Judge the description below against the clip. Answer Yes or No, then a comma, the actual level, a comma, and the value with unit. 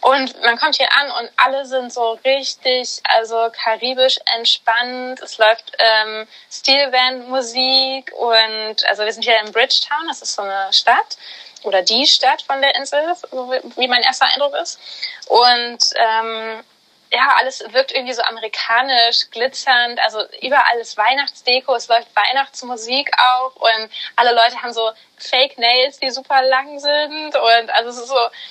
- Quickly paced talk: No, average, 155 wpm